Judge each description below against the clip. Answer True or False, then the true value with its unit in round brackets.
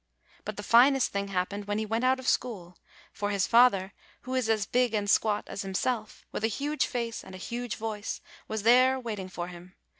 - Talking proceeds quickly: True (215 wpm)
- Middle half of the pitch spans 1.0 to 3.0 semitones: False (3.6 semitones)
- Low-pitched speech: False (220 Hz)